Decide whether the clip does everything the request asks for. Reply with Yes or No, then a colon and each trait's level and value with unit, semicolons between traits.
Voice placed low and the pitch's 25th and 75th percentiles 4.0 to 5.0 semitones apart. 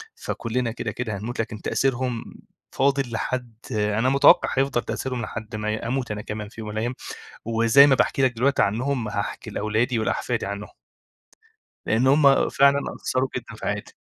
No: low, 120 Hz; average, 3.4 semitones